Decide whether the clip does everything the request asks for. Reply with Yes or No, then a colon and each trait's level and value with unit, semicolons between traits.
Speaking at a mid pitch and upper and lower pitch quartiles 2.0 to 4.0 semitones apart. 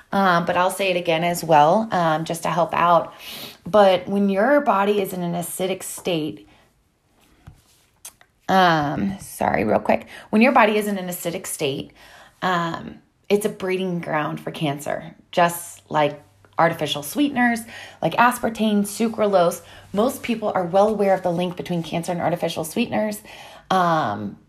Yes: medium, 180 Hz; average, 3.6 semitones